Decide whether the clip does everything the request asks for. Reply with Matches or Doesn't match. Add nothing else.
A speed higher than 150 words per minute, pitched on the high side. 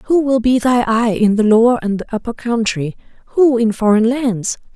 Matches